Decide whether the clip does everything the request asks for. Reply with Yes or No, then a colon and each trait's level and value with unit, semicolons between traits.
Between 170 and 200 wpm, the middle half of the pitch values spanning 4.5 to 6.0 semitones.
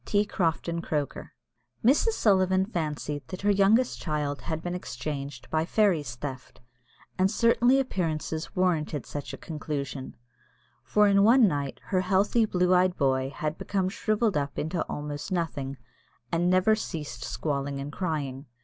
No: average, 145 wpm; average, 5.0 semitones